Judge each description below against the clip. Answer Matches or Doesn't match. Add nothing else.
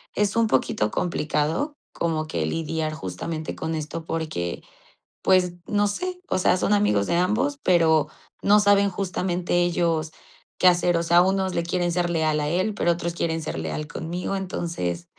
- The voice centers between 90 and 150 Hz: Doesn't match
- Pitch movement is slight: Doesn't match